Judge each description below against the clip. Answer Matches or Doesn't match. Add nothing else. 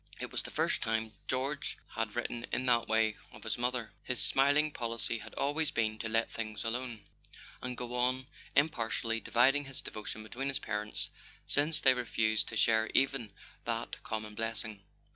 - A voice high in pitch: Doesn't match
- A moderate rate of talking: Matches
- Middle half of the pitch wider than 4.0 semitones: Doesn't match